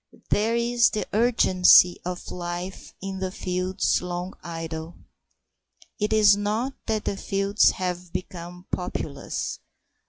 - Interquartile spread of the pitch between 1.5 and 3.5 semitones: Yes, average, 2.9 semitones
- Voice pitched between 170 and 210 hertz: Yes, medium, 185 Hz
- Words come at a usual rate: No, slow, 115 wpm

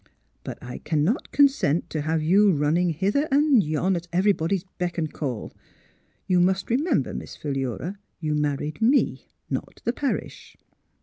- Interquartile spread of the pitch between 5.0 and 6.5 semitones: Yes, average, 5.3 semitones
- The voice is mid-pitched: Yes, medium, 175 Hz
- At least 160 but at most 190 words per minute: No, average, 145 wpm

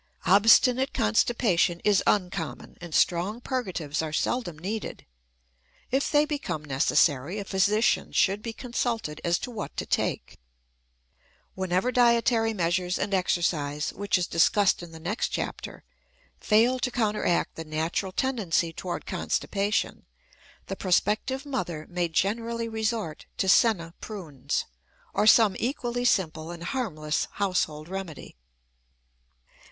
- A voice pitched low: No, high, 195 Hz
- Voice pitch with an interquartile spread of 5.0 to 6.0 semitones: Yes, wide, 5.4 semitones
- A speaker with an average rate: No, slow, 125 wpm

